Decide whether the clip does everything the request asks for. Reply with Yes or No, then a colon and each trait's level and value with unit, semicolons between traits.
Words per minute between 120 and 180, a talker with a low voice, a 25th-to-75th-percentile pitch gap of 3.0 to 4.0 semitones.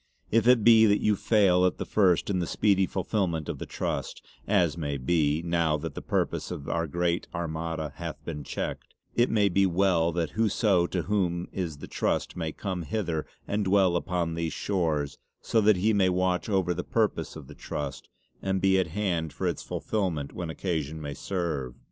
No: average, 195 wpm; very low, 90 Hz; average, 3.4 semitones